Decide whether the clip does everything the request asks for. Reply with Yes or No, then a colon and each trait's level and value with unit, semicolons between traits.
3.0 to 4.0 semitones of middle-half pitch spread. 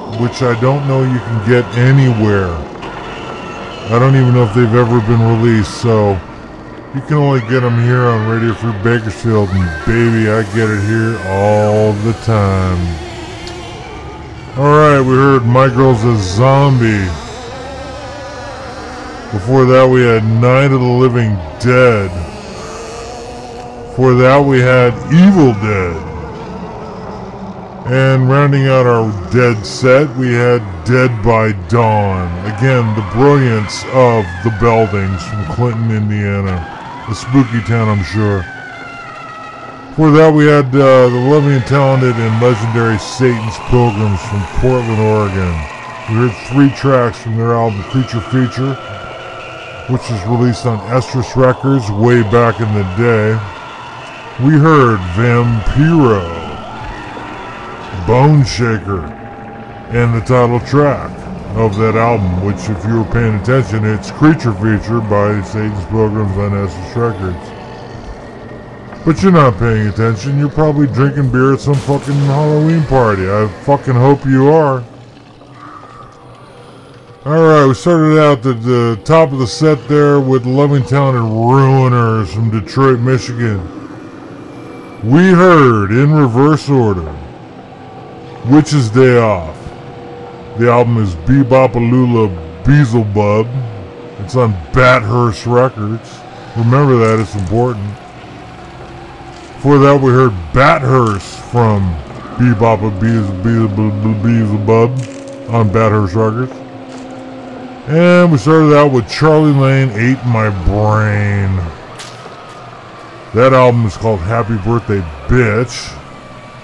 Yes: average, 3.5 semitones